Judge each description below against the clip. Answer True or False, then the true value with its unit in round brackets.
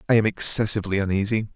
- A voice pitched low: True (105 Hz)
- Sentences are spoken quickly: False (155 wpm)